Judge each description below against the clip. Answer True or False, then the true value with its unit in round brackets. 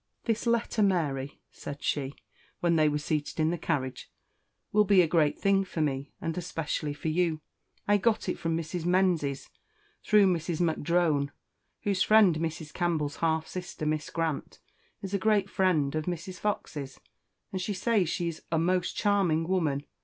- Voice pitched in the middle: True (170 Hz)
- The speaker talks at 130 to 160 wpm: False (170 wpm)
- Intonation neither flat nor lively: True (3.5 semitones)